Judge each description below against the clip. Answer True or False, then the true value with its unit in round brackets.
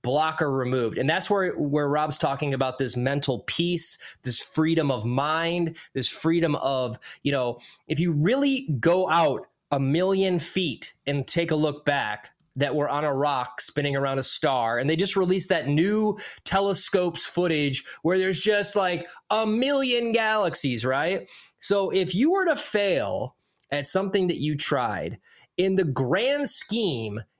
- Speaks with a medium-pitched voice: True (165 Hz)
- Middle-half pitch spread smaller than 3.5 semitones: False (5.1 semitones)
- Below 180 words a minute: True (160 wpm)